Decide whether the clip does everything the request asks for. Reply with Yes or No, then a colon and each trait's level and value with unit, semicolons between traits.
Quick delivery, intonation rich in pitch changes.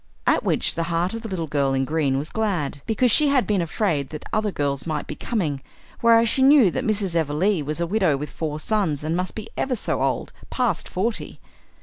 Yes: fast, 220 wpm; wide, 6.4 semitones